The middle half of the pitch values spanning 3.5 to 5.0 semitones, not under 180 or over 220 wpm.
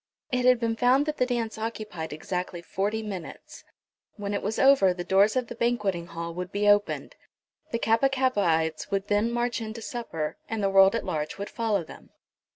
Yes: average, 4.1 semitones; average, 190 wpm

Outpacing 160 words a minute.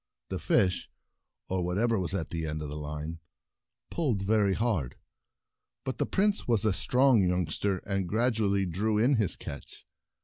Yes: average, 170 wpm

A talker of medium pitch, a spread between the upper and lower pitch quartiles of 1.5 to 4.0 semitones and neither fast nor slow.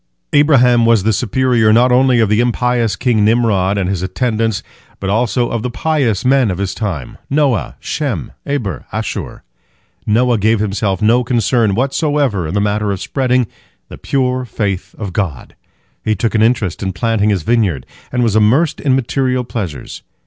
No: low, 115 Hz; average, 3.7 semitones; average, 175 wpm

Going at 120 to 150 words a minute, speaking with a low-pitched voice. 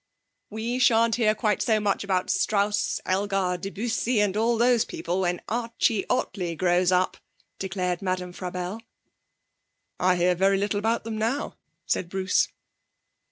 No: average, 140 wpm; high, 200 Hz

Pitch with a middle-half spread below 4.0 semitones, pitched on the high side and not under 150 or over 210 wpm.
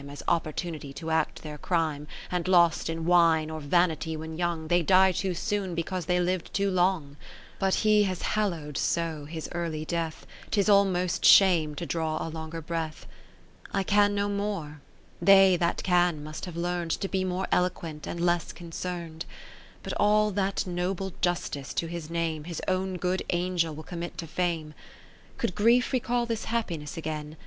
No: average, 2.8 semitones; medium, 175 Hz; average, 175 wpm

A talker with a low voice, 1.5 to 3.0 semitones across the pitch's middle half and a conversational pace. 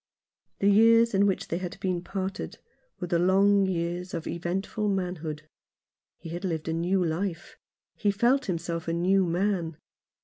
No: medium, 180 Hz; narrow, 2.6 semitones; average, 160 wpm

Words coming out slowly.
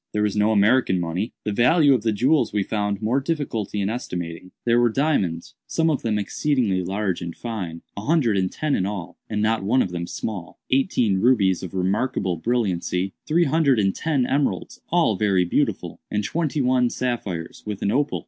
No: average, 180 wpm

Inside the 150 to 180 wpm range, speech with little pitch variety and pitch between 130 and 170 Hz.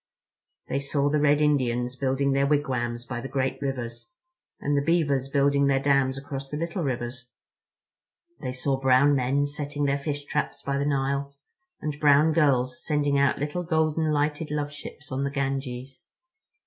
Yes: average, 160 wpm; narrow, 1.7 semitones; medium, 140 Hz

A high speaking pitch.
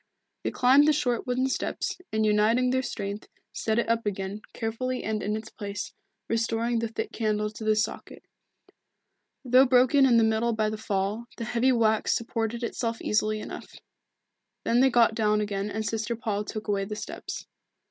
Yes: high, 225 Hz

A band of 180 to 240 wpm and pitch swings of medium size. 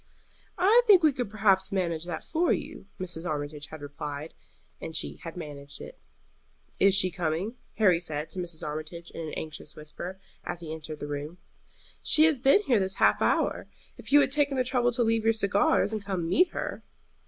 No: average, 200 wpm; wide, 7.1 semitones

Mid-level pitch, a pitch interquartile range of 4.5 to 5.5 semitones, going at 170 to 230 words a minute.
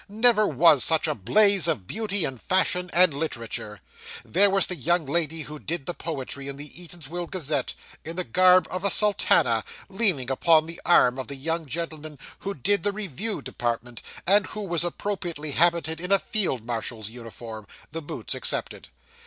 Yes: medium, 165 Hz; average, 5.2 semitones; average, 175 wpm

